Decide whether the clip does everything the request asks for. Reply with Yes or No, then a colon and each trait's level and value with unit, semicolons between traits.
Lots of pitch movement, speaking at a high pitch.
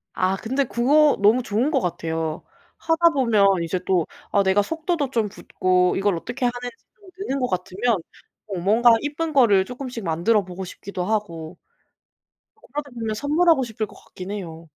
Yes: wide, 6.2 semitones; high, 220 Hz